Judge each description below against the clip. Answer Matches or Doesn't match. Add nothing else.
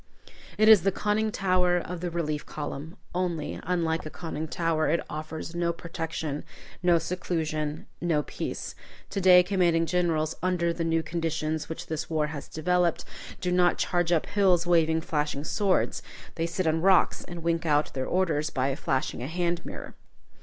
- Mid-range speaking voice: Matches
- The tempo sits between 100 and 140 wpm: Doesn't match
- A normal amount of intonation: Doesn't match